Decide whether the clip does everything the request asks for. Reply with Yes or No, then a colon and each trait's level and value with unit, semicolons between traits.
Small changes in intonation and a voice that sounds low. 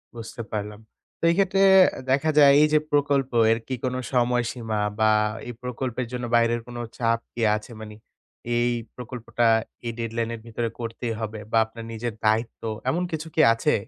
Yes: narrow, 2.0 semitones; low, 120 Hz